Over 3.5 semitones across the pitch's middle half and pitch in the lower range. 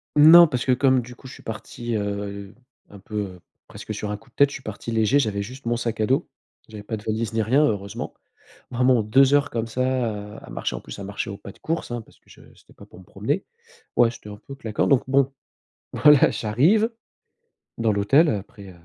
Yes: average, 4.3 semitones; low, 115 Hz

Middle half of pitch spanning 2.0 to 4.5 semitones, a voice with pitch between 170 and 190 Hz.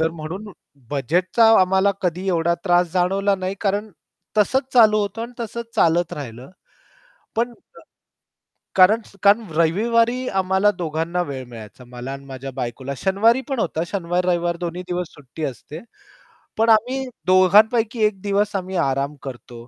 No: average, 4.9 semitones; medium, 185 Hz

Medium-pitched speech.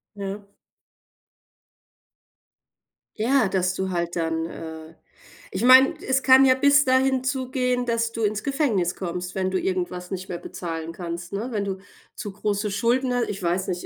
No: high, 200 Hz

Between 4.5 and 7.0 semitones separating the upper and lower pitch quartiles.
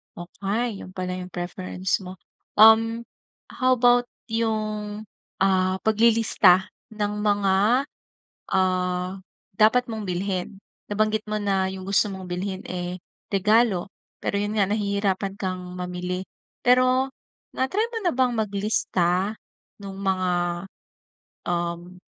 No: average, 2.9 semitones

